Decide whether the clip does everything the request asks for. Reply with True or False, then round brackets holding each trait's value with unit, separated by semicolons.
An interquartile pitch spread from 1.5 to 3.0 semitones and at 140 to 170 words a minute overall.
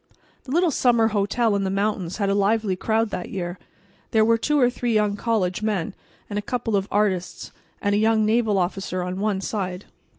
False (2.7 semitones; 200 wpm)